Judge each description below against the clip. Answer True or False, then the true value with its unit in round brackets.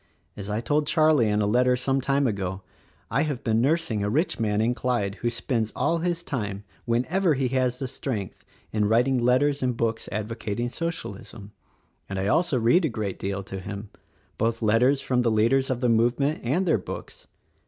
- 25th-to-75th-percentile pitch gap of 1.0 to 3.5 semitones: False (4.1 semitones)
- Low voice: True (120 Hz)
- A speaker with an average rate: True (195 wpm)